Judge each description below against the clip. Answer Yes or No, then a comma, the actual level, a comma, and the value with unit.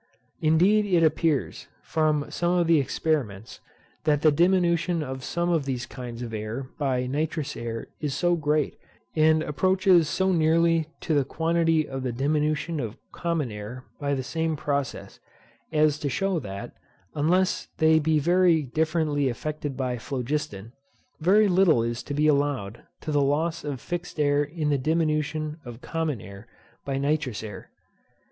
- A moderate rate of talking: Yes, average, 155 wpm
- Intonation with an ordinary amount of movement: Yes, average, 3.6 semitones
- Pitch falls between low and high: Yes, medium, 150 Hz